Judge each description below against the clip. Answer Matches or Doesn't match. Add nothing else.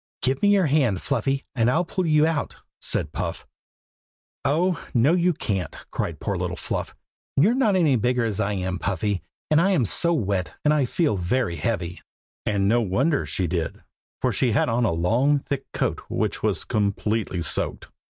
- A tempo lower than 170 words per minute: Doesn't match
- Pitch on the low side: Matches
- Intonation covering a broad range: Matches